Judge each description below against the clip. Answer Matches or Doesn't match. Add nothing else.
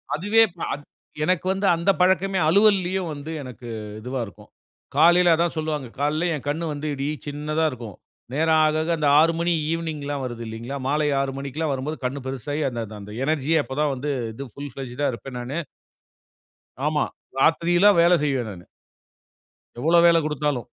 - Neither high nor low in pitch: Matches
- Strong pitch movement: Doesn't match